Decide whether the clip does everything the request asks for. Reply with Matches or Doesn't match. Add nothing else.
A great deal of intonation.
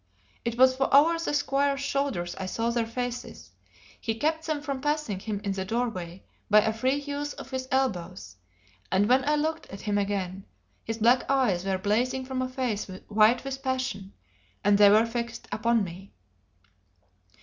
Doesn't match